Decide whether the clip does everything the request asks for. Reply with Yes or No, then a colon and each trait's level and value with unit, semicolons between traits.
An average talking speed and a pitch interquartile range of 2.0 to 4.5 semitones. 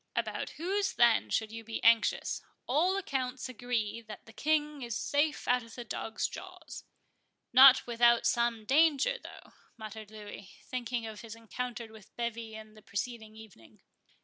Yes: average, 150 wpm; average, 2.8 semitones